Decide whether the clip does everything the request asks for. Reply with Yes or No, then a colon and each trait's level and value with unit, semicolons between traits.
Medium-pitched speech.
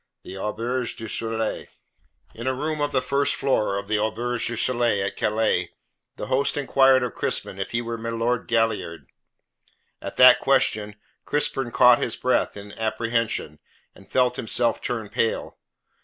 No: low, 115 Hz